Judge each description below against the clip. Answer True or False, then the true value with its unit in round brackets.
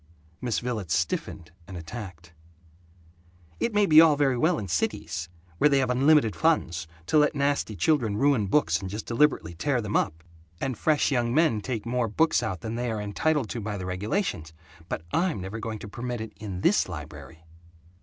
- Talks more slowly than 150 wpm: False (185 wpm)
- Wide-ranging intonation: True (7.0 semitones)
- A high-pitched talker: False (115 Hz)